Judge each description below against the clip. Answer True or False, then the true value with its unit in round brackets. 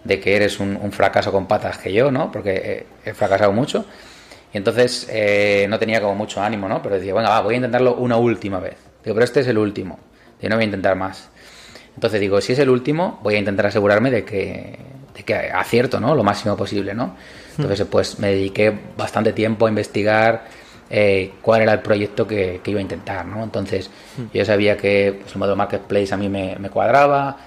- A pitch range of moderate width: False (2.1 semitones)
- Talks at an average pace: False (215 wpm)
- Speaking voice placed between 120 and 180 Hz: False (105 Hz)